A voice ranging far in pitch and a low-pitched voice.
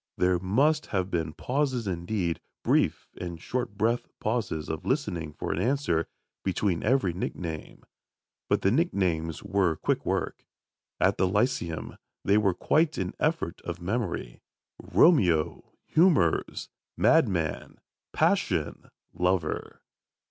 Yes: wide, 6.5 semitones; very low, 95 Hz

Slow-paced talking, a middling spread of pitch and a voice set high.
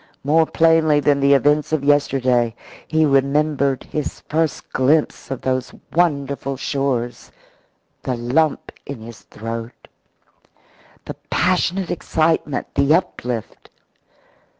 No: slow, 105 wpm; average, 3.4 semitones; medium, 140 Hz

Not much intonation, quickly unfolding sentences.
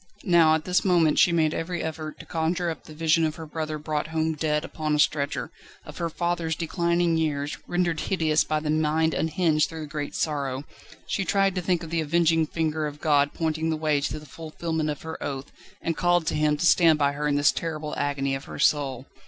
Yes: narrow, 1.7 semitones; fast, 220 wpm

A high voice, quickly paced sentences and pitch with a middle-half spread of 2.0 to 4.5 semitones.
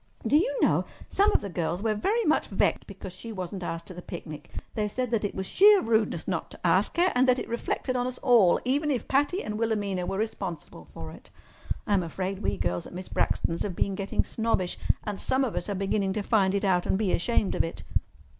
No: high, 205 Hz; fast, 230 wpm; average, 5.0 semitones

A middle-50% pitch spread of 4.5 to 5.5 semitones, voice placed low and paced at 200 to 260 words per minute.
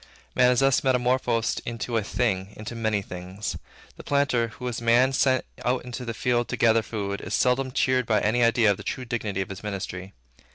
No: average, 3.1 semitones; low, 115 Hz; fast, 205 wpm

